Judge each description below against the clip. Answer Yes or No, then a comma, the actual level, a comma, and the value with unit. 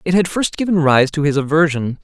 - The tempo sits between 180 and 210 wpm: No, fast, 235 wpm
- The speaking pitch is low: No, medium, 160 Hz